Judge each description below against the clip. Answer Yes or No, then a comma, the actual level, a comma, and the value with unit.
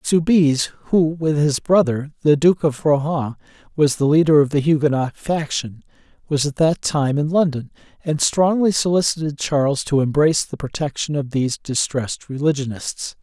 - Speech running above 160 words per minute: No, average, 155 wpm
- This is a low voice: No, medium, 150 Hz